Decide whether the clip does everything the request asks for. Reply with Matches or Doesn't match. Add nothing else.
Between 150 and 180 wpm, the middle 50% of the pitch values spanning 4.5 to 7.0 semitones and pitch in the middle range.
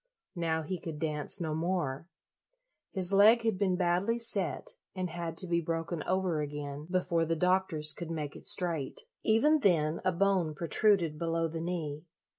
Doesn't match